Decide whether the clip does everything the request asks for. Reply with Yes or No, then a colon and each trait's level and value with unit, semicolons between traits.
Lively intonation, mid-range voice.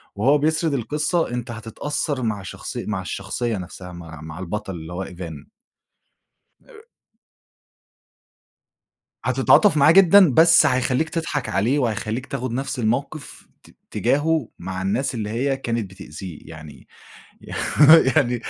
No: wide, 7.2 semitones; low, 120 Hz